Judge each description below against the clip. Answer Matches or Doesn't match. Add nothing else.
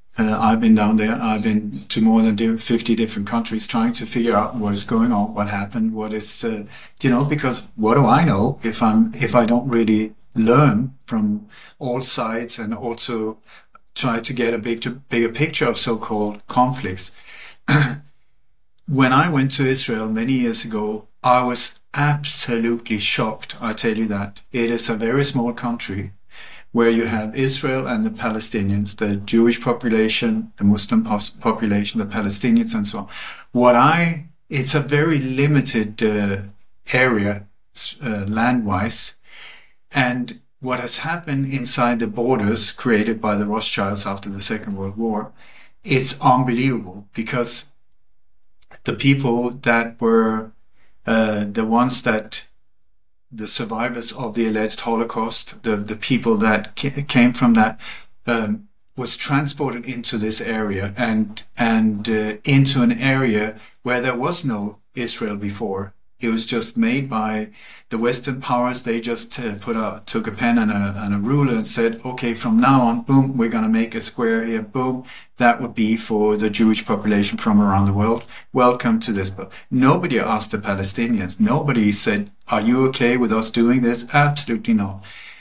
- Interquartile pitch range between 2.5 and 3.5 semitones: Matches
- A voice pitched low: Matches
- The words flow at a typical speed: Matches